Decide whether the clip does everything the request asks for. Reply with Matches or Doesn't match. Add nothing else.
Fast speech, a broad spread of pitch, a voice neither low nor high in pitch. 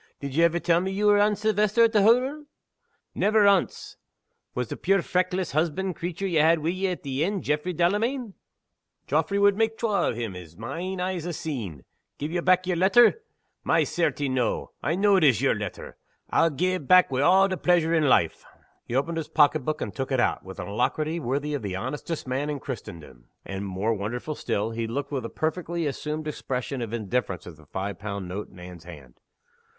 Matches